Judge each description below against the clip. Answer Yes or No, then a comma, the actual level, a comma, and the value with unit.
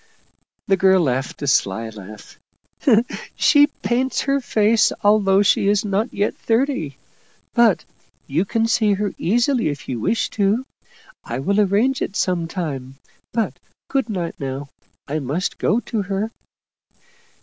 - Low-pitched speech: No, high, 200 Hz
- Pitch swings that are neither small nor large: No, wide, 7.0 semitones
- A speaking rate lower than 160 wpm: Yes, average, 150 wpm